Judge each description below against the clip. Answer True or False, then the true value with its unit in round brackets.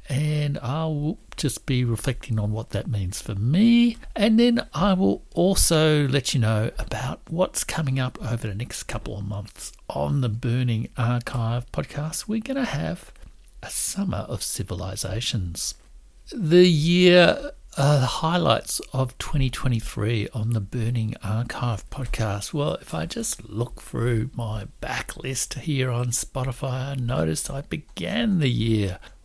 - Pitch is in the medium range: False (125 Hz)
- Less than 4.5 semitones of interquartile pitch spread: False (5.2 semitones)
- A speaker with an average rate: True (150 wpm)